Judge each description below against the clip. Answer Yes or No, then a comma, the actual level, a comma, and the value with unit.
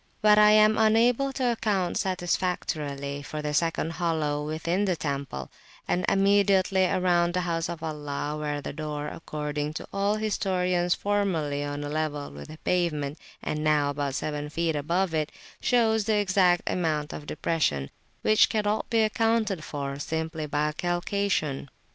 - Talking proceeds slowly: No, average, 155 wpm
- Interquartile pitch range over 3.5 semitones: Yes, average, 4.9 semitones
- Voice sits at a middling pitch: Yes, medium, 165 Hz